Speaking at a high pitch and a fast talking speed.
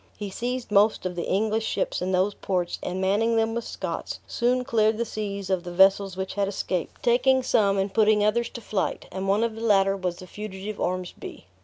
Yes: high, 205 Hz; fast, 210 wpm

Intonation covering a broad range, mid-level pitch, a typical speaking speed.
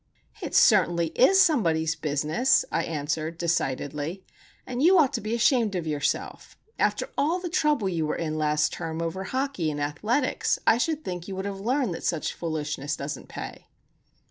Yes: wide, 8.0 semitones; medium, 175 Hz; average, 170 wpm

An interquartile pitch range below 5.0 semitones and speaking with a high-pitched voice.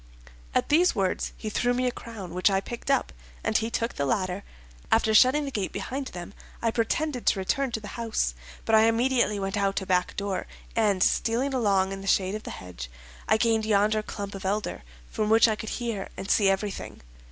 Yes: average, 3.1 semitones; high, 215 Hz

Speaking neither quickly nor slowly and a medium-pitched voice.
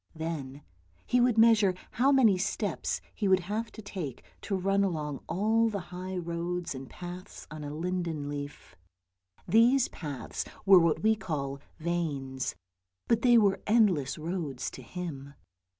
Yes: average, 150 wpm; medium, 180 Hz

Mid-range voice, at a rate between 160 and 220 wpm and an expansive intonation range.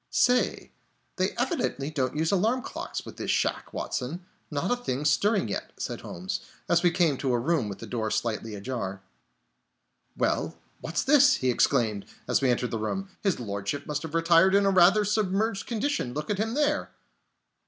Yes: medium, 160 Hz; average, 180 wpm; wide, 8.4 semitones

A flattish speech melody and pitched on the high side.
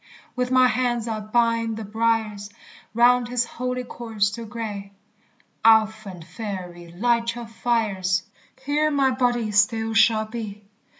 Yes: narrow, 2.3 semitones; high, 225 Hz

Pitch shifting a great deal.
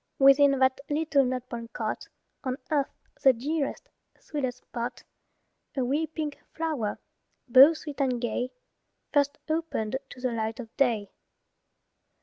No: average, 3.1 semitones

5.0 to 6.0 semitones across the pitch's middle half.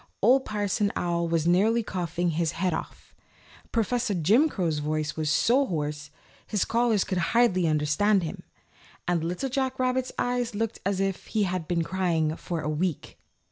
Yes: wide, 5.5 semitones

